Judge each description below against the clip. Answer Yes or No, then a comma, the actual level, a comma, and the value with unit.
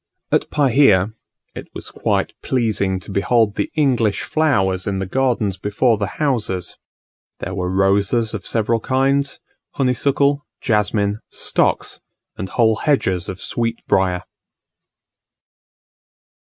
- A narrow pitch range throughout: No, average, 5.1 semitones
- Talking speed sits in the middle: No, slow, 115 wpm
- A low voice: Yes, low, 110 Hz